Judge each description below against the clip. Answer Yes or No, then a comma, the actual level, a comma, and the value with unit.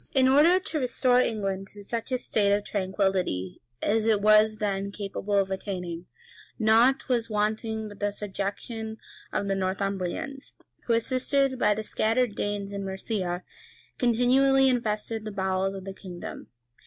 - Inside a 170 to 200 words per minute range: No, average, 155 wpm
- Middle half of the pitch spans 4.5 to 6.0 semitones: No, average, 3.2 semitones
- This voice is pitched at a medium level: No, high, 210 Hz